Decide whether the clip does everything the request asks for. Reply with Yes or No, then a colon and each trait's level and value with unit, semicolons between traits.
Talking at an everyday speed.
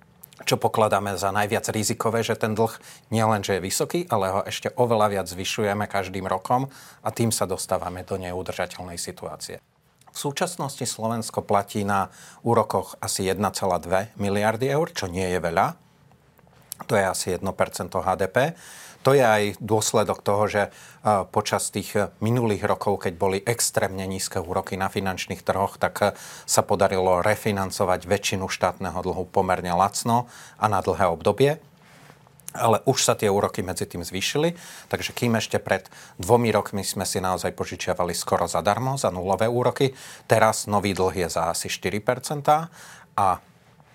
Yes: average, 145 wpm